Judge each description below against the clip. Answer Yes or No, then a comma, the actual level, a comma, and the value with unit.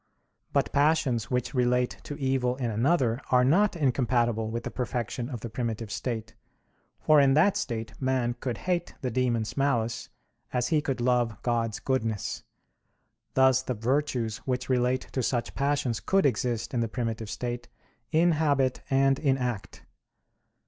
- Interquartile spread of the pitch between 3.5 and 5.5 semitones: No, narrow, 2.6 semitones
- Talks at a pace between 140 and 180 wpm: Yes, average, 155 wpm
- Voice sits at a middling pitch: No, low, 125 Hz